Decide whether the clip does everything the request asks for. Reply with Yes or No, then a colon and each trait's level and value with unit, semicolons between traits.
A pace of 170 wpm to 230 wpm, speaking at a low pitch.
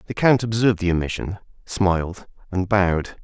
No: average, 150 wpm; very low, 95 Hz